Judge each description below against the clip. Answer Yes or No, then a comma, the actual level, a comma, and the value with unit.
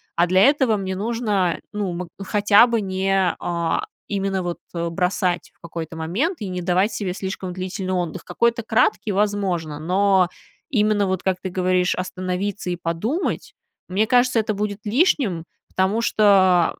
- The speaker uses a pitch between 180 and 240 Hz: Yes, high, 190 Hz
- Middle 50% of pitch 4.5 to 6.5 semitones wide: No, average, 2.8 semitones